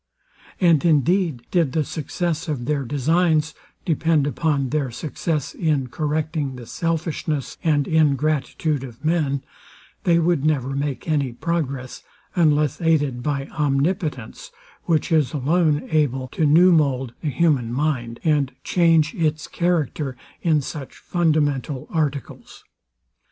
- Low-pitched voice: No, medium, 150 Hz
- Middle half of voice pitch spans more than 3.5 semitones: No, average, 3.0 semitones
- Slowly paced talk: Yes, slow, 125 wpm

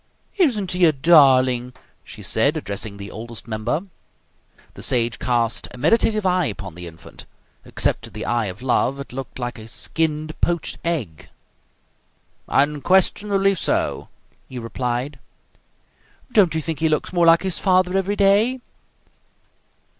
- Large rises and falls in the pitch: Yes, wide, 7.3 semitones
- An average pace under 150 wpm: Yes, average, 140 wpm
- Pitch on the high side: No, medium, 145 Hz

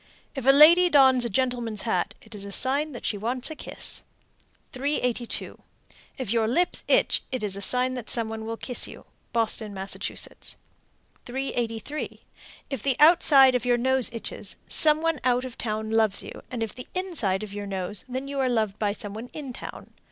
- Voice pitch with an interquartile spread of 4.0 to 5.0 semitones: No, average, 3.6 semitones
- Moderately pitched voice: No, high, 245 Hz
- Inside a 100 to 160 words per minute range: No, average, 190 wpm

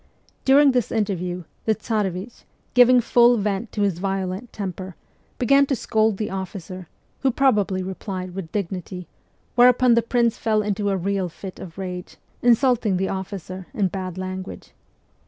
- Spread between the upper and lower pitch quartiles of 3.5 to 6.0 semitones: Yes, average, 3.9 semitones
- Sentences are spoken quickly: No, average, 150 wpm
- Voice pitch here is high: Yes, high, 200 Hz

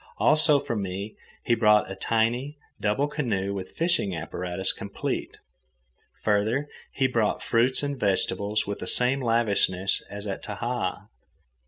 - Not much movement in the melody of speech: No, average, 4.3 semitones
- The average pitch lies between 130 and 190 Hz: No, low, 110 Hz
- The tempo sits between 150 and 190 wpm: No, slow, 135 wpm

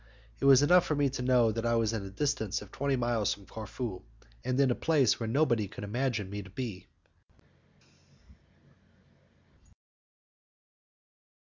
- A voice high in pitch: No, low, 120 Hz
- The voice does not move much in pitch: No, average, 4.2 semitones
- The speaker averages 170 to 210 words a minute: No, average, 150 wpm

